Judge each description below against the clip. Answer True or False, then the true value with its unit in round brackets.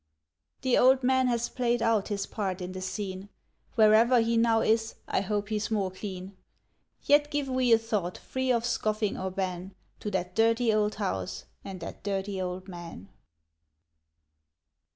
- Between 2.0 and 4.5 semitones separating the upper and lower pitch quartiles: True (3.7 semitones)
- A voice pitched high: True (210 Hz)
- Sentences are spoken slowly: False (160 wpm)